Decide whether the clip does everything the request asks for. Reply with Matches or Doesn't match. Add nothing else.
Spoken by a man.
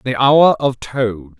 Matches